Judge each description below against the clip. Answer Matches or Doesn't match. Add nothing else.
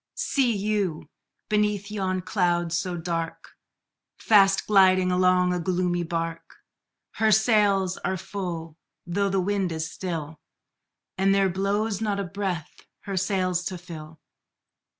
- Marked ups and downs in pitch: Doesn't match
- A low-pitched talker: Doesn't match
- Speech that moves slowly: Matches